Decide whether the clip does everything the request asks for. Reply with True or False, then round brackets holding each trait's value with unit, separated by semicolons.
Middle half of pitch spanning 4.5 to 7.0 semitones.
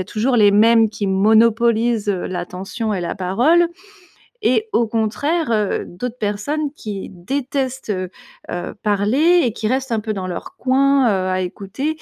True (4.9 semitones)